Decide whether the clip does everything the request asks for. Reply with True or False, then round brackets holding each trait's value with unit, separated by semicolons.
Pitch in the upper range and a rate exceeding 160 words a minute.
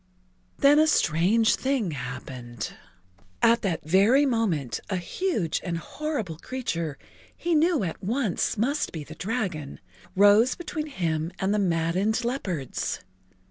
False (200 Hz; 135 wpm)